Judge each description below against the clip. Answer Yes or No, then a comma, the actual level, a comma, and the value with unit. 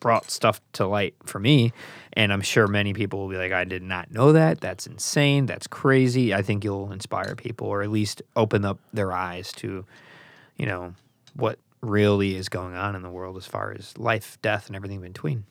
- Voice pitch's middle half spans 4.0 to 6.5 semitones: No, average, 3.3 semitones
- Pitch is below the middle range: Yes, low, 105 Hz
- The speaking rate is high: Yes, fast, 215 wpm